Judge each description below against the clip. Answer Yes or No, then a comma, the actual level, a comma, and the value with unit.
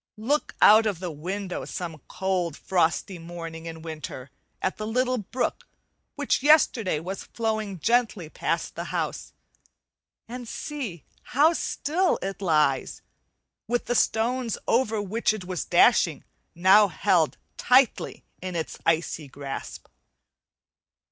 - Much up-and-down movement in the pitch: Yes, wide, 5.9 semitones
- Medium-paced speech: No, slow, 125 wpm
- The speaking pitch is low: No, high, 195 Hz